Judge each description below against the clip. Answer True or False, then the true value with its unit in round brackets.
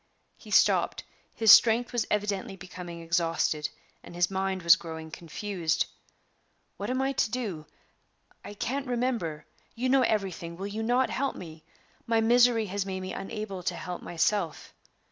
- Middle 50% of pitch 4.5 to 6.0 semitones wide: True (5.2 semitones)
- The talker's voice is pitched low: False (195 Hz)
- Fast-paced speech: False (155 wpm)